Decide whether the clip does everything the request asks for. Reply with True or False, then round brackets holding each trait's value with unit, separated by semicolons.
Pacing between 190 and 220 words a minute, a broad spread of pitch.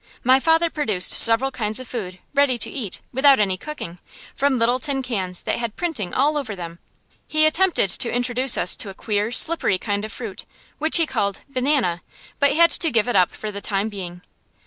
True (200 wpm; 6.0 semitones)